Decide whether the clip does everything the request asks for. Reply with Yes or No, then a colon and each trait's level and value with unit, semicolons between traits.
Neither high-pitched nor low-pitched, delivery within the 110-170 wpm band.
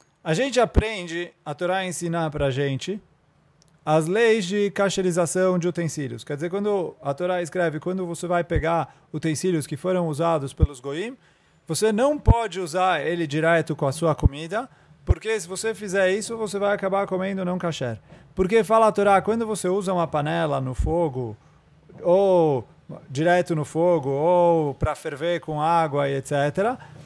Yes: medium, 170 Hz; average, 160 wpm